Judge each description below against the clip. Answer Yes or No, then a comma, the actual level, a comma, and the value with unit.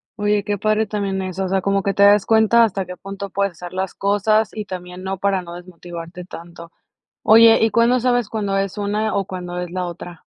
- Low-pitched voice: No, high, 195 Hz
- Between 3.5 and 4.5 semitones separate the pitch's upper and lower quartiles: No, narrow, 2.5 semitones